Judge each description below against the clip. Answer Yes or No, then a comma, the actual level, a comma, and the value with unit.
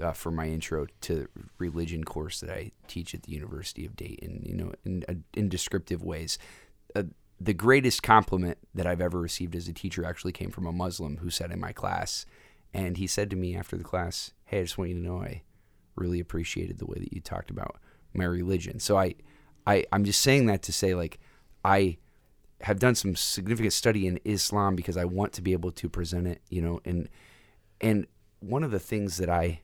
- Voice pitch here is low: Yes, very low, 90 Hz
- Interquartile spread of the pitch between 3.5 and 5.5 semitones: No, average, 2.8 semitones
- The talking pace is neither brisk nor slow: No, fast, 215 wpm